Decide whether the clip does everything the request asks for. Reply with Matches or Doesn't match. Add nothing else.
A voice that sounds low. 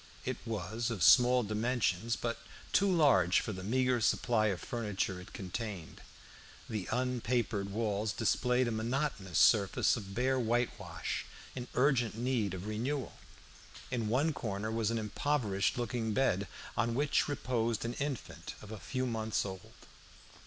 Matches